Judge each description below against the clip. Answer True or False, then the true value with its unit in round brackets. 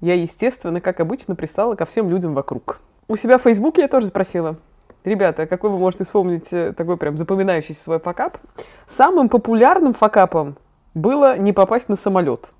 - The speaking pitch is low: False (190 Hz)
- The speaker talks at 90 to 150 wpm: False (160 wpm)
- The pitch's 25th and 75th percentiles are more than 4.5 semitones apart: True (5.2 semitones)